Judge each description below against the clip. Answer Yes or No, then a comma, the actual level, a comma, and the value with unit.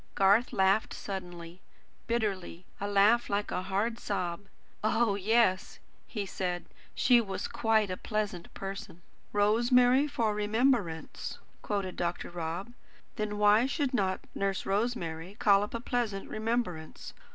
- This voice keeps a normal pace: No, slow, 130 wpm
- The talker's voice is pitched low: No, high, 205 Hz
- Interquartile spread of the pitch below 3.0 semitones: No, average, 3.4 semitones